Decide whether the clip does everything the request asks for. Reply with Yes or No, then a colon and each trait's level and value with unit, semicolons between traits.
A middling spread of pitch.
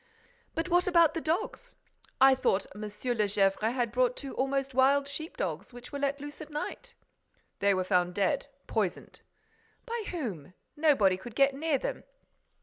No: wide, 6.4 semitones